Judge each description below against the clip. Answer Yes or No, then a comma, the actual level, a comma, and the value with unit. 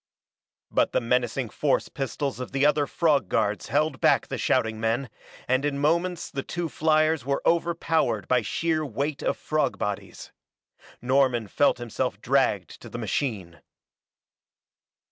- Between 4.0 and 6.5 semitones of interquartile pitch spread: Yes, average, 4.3 semitones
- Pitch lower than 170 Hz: Yes, medium, 140 Hz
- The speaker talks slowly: No, average, 145 wpm